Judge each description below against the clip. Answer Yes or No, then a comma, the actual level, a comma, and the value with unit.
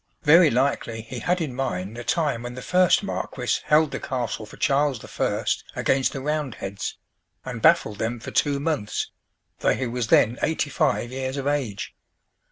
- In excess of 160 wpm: Yes, average, 175 wpm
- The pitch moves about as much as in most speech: Yes, average, 4.0 semitones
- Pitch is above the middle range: No, low, 130 Hz